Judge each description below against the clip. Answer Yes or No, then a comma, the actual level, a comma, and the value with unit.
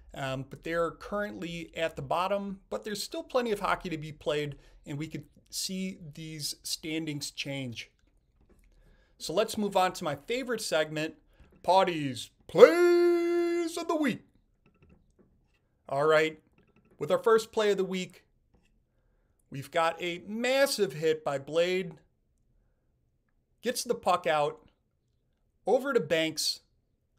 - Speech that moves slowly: Yes, slow, 130 wpm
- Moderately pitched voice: Yes, medium, 165 Hz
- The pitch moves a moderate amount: No, wide, 5.9 semitones